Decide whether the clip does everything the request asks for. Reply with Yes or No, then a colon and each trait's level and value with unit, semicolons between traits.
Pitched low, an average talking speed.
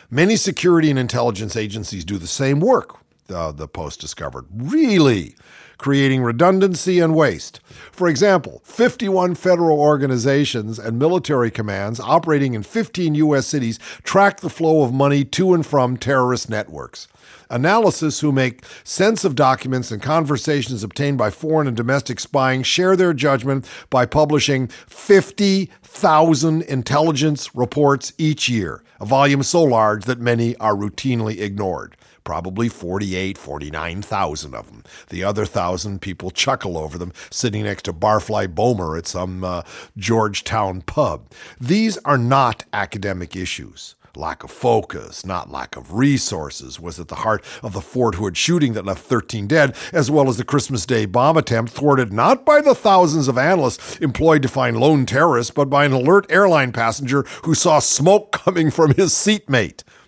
Yes: low, 130 Hz; average, 155 wpm